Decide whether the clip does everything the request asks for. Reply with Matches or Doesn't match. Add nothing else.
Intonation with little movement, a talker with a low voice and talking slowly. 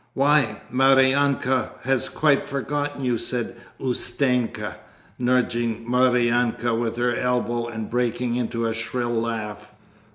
Matches